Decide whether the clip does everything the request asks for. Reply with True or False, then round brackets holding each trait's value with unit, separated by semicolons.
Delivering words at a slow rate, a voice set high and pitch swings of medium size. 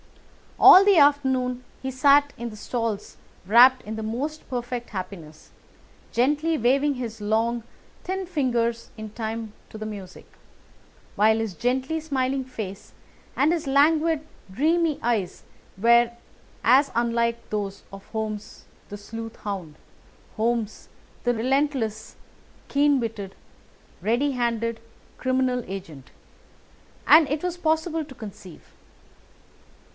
True (120 wpm; 240 Hz; 4.5 semitones)